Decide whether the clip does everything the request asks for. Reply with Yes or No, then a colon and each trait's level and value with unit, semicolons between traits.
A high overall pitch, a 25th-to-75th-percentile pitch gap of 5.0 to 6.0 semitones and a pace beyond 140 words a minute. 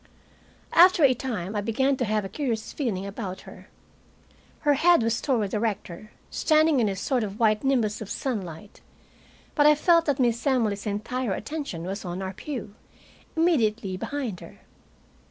Yes: high, 230 Hz; wide, 5.4 semitones; average, 165 wpm